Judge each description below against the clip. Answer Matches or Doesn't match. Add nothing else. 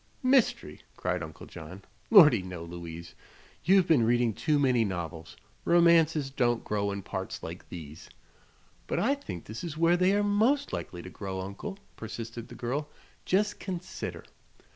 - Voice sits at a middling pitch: Doesn't match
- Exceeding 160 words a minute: Doesn't match